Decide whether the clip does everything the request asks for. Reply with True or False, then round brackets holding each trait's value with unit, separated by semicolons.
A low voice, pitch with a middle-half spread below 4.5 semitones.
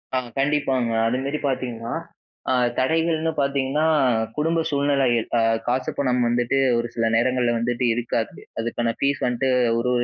True (130 Hz; 2.8 semitones)